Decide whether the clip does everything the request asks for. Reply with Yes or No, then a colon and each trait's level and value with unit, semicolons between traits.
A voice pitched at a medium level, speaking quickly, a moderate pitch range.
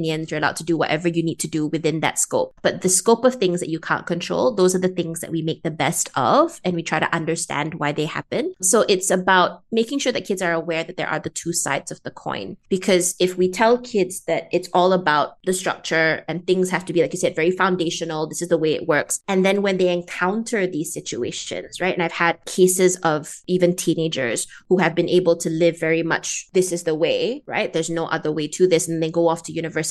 No: medium, 170 Hz; fast, 250 wpm; narrow, 2.2 semitones